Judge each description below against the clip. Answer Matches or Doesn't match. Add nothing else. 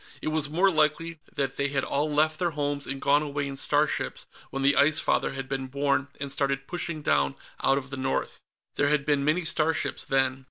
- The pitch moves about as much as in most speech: Doesn't match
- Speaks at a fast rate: Matches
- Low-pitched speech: Doesn't match